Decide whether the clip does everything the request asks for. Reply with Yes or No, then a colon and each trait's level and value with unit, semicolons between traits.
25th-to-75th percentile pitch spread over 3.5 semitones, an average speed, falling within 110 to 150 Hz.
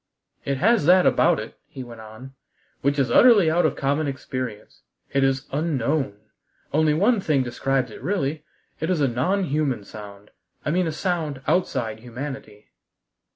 Yes: average, 4.3 semitones; average, 160 wpm; medium, 140 Hz